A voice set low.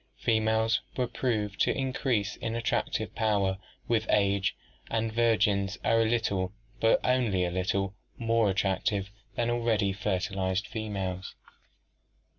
Yes: low, 105 Hz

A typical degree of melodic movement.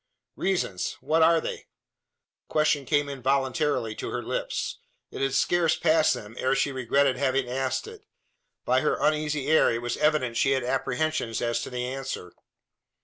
Yes: average, 3.5 semitones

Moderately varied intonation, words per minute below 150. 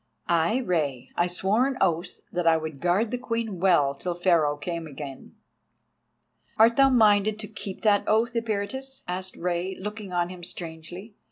No: average, 4.4 semitones; average, 165 wpm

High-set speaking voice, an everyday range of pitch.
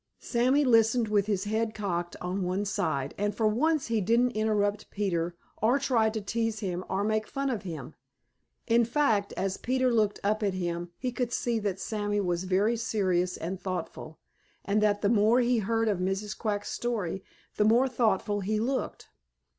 Yes: high, 210 Hz; average, 3.3 semitones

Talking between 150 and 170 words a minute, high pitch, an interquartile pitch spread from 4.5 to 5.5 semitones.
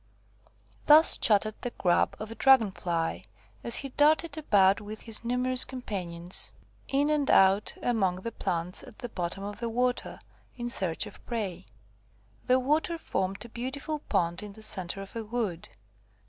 Yes: average, 160 wpm; high, 220 Hz; average, 4.9 semitones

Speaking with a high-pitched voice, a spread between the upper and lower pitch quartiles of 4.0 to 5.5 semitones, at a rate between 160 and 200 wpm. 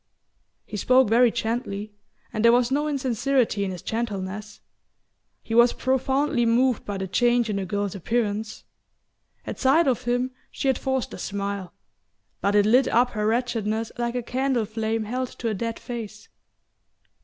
No: high, 230 Hz; average, 3.0 semitones; average, 165 wpm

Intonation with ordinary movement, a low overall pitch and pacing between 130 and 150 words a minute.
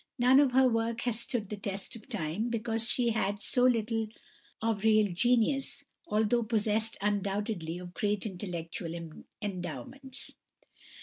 No: average, 3.1 semitones; high, 220 Hz; average, 140 wpm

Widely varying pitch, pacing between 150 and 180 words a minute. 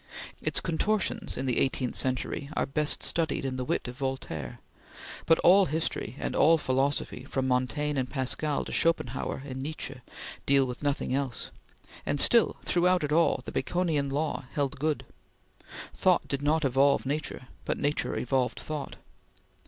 No: average, 2.9 semitones; average, 155 wpm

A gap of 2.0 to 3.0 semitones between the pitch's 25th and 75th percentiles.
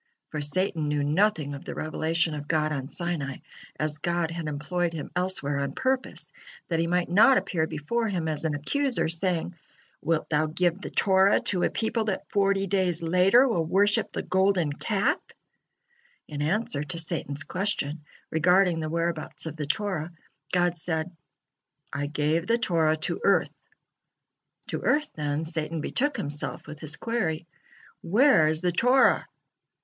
No: average, 4.0 semitones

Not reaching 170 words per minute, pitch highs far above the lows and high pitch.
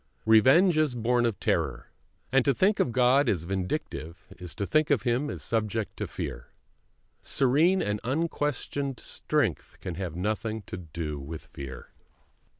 No: average, 155 wpm; wide, 7.5 semitones; low, 115 Hz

